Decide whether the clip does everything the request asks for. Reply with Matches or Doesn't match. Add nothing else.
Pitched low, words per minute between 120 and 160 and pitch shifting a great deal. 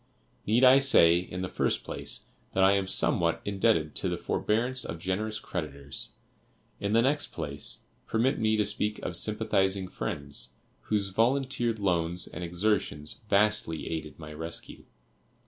Doesn't match